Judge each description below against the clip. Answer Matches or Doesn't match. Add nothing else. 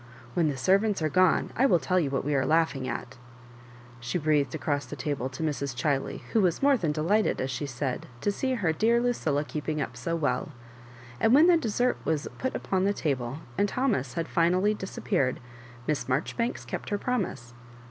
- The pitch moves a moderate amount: Doesn't match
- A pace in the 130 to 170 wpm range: Doesn't match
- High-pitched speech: Doesn't match